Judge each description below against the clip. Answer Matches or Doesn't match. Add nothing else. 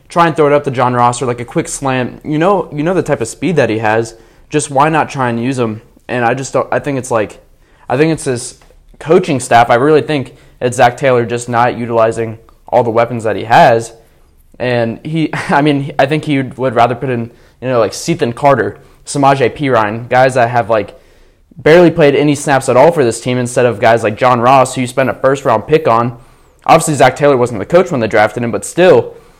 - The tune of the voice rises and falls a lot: Doesn't match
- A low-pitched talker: Matches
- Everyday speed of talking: Doesn't match